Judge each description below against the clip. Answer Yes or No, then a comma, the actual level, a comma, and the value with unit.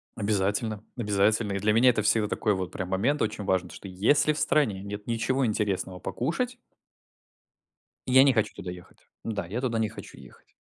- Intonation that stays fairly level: No, average, 3.6 semitones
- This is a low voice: Yes, low, 105 Hz